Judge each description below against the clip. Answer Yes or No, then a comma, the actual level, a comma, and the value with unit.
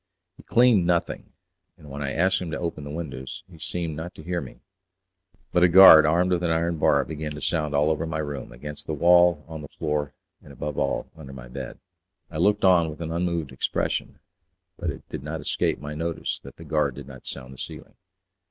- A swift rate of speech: Yes, fast, 215 wpm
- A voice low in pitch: Yes, very low, 80 Hz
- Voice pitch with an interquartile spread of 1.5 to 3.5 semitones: Yes, average, 2.8 semitones